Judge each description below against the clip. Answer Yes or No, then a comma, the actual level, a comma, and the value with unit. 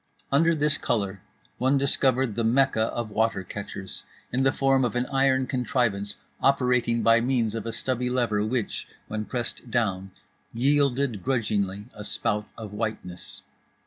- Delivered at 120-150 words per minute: Yes, average, 145 wpm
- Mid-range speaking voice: No, low, 120 Hz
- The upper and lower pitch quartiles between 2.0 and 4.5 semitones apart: Yes, average, 3.8 semitones